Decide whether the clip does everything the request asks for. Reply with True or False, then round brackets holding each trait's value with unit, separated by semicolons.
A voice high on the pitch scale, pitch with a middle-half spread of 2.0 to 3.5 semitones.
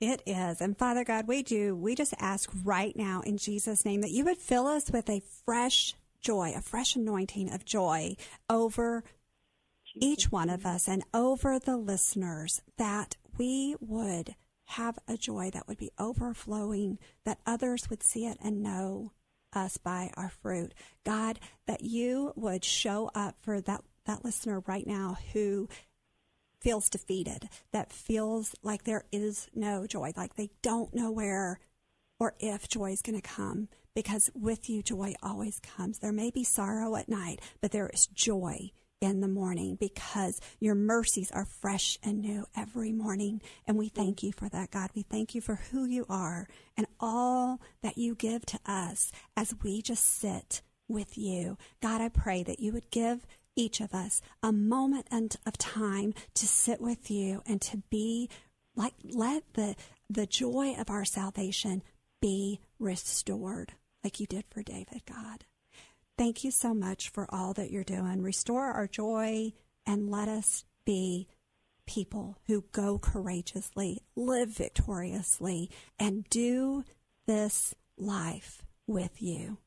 True (210 Hz; 2.6 semitones)